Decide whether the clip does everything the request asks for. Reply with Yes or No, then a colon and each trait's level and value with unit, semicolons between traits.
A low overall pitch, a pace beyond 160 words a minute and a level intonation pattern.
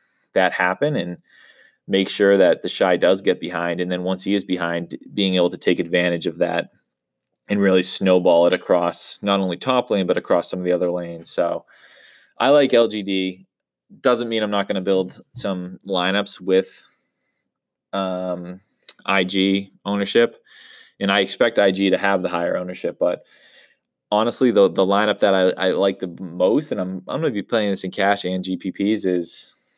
Yes: very low, 95 Hz; average, 180 wpm; narrow, 1.8 semitones